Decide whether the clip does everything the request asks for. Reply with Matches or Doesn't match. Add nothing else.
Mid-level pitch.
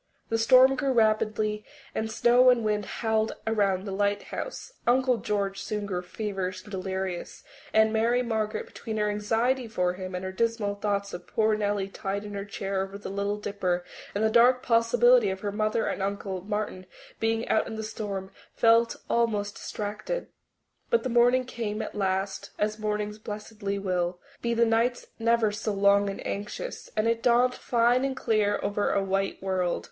Doesn't match